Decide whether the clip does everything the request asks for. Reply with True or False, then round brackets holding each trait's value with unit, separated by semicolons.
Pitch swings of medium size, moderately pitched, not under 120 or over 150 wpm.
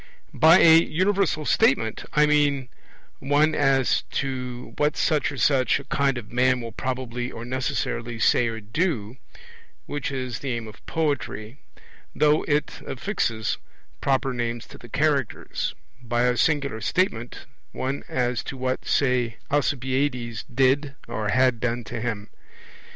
False (3.3 semitones; 130 Hz; 140 wpm)